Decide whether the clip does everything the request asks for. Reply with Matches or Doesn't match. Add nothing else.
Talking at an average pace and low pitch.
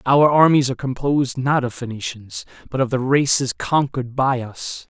Matches